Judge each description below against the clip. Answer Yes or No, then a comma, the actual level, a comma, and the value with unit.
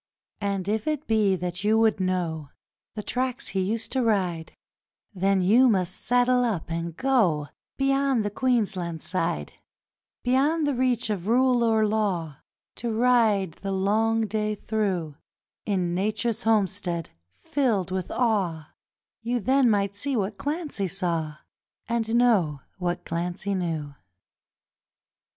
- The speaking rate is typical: No, slow, 130 wpm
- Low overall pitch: No, high, 205 Hz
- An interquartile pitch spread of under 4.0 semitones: No, average, 4.7 semitones